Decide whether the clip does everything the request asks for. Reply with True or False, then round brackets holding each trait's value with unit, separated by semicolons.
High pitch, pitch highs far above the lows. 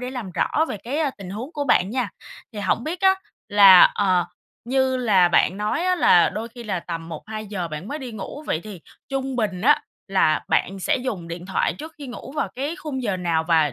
True (215 Hz; 6.4 semitones)